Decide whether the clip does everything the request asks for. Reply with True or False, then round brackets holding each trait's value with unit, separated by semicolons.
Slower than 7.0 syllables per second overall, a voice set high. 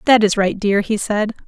True (4.9 syllables/s; 210 Hz)